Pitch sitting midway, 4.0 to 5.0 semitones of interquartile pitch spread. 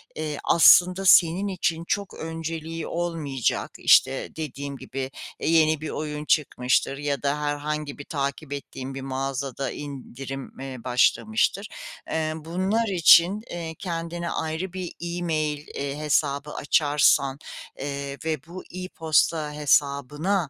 No: medium, 150 Hz; average, 3.1 semitones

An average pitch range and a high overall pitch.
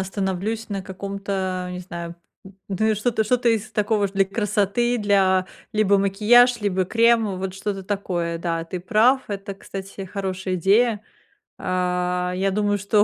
No: narrow, 2.3 semitones; high, 195 Hz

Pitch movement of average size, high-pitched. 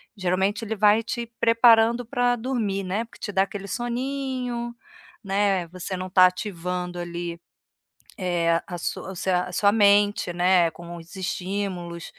Yes: average, 4.1 semitones; high, 195 Hz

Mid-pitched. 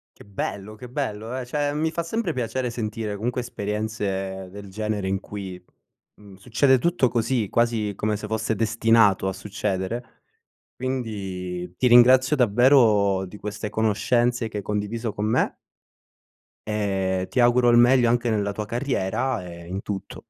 No: low, 110 Hz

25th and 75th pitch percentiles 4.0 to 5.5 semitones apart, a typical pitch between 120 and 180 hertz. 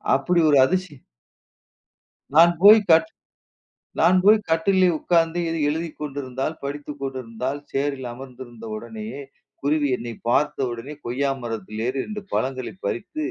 Yes: average, 4.3 semitones; medium, 140 Hz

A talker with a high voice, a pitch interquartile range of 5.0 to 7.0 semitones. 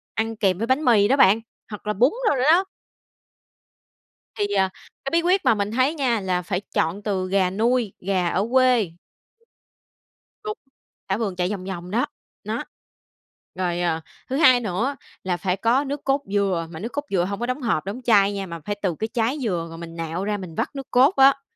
Yes: high, 205 Hz; wide, 5.5 semitones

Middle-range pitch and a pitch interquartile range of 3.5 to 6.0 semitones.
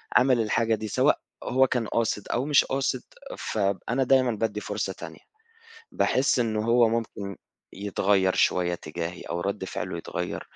No: low, 110 Hz; average, 3.8 semitones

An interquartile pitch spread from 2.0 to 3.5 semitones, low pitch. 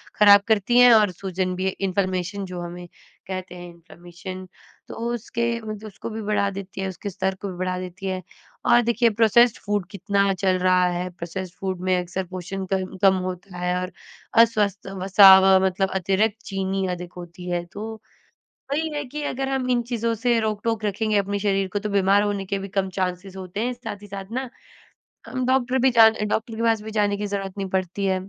No: average, 2.8 semitones; high, 195 Hz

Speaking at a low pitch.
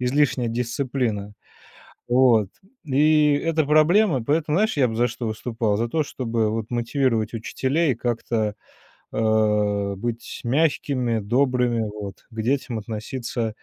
Yes: low, 120 Hz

